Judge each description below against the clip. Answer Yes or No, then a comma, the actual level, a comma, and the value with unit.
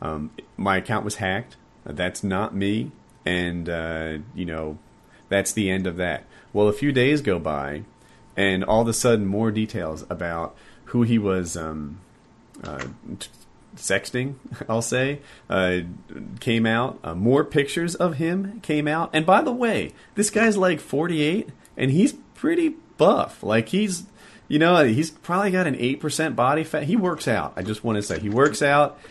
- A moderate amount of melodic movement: No, wide, 8.9 semitones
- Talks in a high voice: No, low, 115 Hz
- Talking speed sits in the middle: Yes, average, 170 wpm